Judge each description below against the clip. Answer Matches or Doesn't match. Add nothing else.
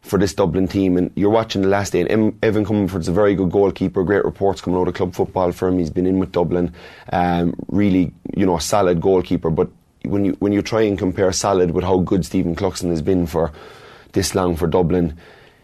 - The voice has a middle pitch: Doesn't match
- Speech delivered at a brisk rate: Matches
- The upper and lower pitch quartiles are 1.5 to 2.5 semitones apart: Matches